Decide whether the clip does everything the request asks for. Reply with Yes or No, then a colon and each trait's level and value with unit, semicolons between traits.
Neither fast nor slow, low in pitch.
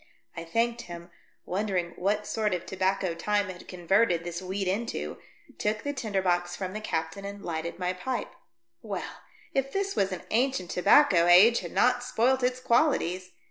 No: average, 170 wpm; high, 195 Hz